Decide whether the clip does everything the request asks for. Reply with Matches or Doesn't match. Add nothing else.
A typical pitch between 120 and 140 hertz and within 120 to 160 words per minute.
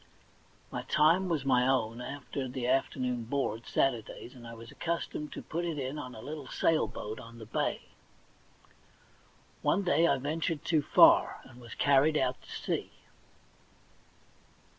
Matches